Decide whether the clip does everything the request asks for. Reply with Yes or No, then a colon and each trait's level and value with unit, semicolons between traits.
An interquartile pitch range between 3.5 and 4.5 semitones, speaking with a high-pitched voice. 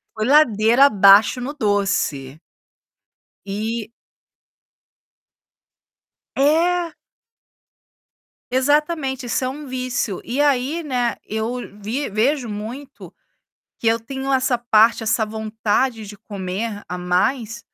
Yes: average, 4.1 semitones; high, 235 Hz